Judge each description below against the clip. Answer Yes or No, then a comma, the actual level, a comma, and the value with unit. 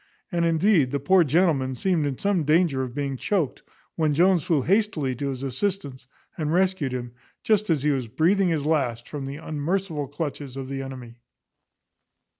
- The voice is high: No, medium, 150 Hz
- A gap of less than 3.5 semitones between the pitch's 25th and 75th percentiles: No, average, 4.6 semitones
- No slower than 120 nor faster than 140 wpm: No, average, 175 wpm